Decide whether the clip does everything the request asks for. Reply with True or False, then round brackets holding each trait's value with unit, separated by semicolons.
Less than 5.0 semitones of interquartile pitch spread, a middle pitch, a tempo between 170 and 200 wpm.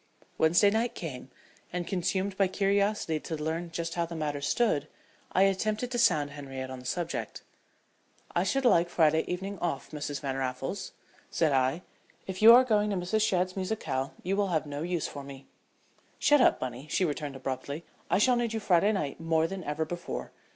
False (5.3 semitones; 170 Hz; 185 wpm)